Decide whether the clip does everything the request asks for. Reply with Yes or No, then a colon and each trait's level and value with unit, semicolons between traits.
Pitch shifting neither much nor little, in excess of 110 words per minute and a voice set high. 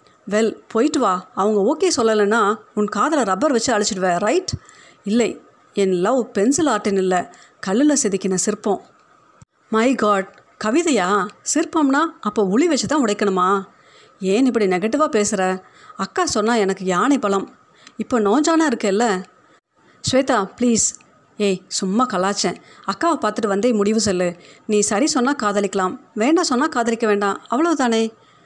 Yes: average, 4.9 semitones; fast, 130 wpm; high, 215 Hz